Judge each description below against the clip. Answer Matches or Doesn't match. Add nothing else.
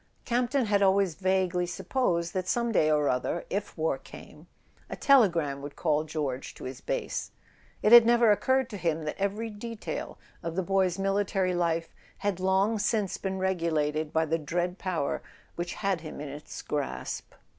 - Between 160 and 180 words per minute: Matches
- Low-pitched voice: Doesn't match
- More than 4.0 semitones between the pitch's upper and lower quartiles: Matches